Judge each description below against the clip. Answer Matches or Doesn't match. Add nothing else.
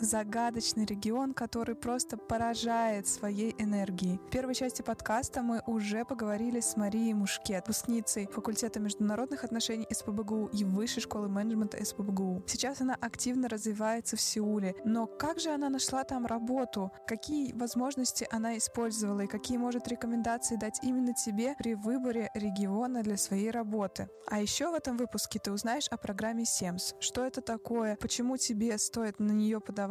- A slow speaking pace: Doesn't match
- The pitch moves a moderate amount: Doesn't match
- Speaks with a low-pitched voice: Doesn't match